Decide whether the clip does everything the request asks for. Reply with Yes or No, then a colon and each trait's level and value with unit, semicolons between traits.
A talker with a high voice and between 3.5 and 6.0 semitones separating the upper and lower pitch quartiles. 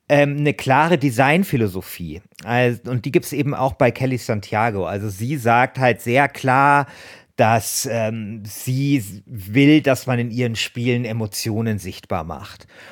No: low, 120 Hz; average, 4.1 semitones